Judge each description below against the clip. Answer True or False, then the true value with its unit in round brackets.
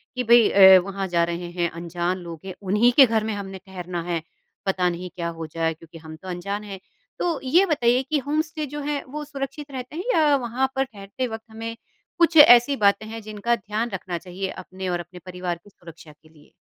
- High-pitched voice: True (200 Hz)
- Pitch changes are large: True (6.4 semitones)